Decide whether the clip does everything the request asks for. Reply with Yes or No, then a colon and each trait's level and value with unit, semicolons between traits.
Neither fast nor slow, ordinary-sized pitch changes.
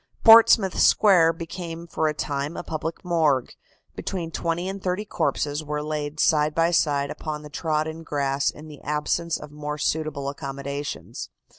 No: average, 155 wpm; narrow, 2.3 semitones